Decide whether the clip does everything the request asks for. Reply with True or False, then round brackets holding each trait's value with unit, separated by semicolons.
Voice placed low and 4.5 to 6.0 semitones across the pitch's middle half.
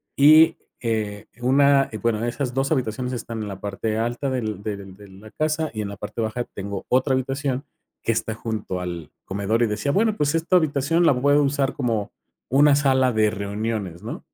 True (120 Hz; 4.8 semitones)